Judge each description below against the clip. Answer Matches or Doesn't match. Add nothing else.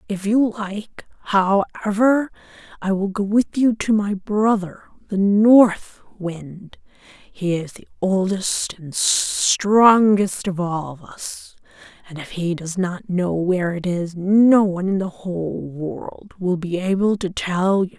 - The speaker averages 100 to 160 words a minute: Matches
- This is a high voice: Matches